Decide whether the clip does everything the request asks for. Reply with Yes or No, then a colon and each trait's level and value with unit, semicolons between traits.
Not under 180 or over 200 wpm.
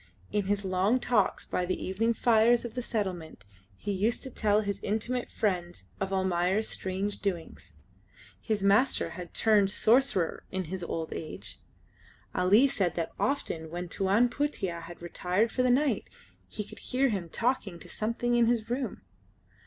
No: average, 160 wpm